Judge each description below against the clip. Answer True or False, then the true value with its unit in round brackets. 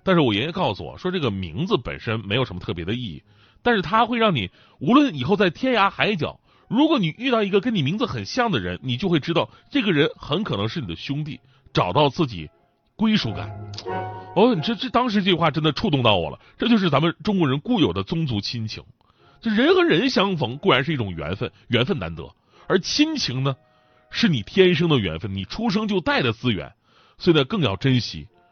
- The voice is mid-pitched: True (155 Hz)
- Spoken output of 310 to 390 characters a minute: True (320 characters per minute)